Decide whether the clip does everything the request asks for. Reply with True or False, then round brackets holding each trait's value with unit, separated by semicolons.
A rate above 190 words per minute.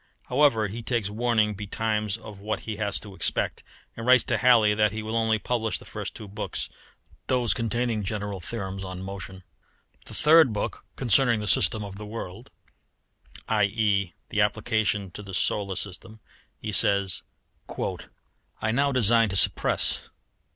False (155 wpm)